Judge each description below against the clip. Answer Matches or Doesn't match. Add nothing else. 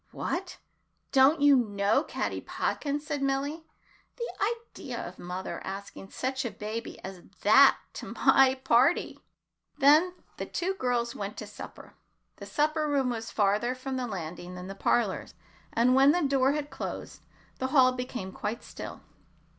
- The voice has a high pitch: Matches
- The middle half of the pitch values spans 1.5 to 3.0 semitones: Doesn't match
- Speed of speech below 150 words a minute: Doesn't match